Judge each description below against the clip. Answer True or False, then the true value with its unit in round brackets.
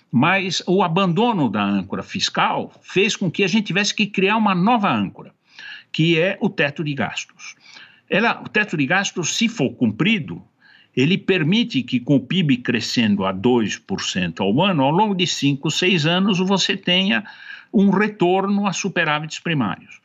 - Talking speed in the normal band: True (165 wpm)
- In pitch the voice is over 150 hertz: True (190 Hz)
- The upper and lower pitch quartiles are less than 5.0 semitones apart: True (4.4 semitones)